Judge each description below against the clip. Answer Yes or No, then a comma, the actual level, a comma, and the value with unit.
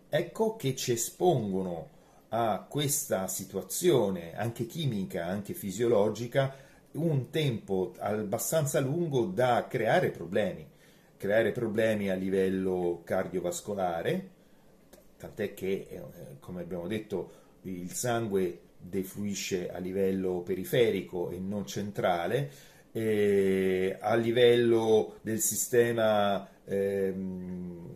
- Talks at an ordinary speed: No, slow, 95 wpm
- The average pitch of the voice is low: Yes, low, 105 Hz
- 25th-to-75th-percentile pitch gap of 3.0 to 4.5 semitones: Yes, average, 4.2 semitones